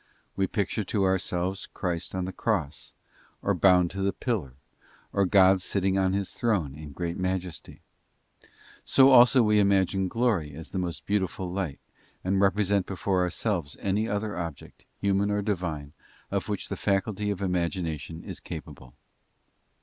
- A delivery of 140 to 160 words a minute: Yes, average, 150 wpm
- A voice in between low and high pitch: No, very low, 95 Hz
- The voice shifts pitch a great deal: No, narrow, 2.5 semitones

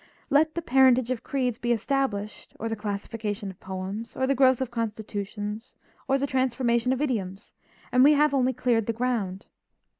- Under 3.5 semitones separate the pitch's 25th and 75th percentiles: No, average, 3.8 semitones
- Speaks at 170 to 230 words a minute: Yes, average, 175 wpm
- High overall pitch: Yes, high, 240 Hz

